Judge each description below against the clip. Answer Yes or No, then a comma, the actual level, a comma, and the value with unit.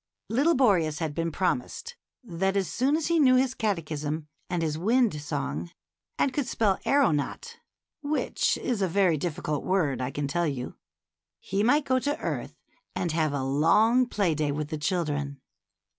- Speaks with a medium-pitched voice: Yes, medium, 175 Hz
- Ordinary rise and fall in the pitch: No, wide, 8.5 semitones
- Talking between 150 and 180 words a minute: Yes, average, 175 wpm